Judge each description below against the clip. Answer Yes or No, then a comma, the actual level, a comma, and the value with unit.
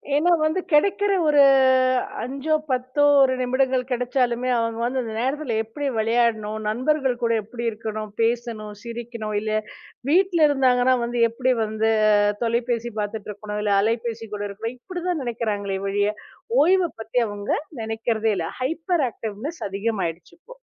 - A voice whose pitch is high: Yes, high, 235 Hz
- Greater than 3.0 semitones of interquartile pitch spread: Yes, average, 3.6 semitones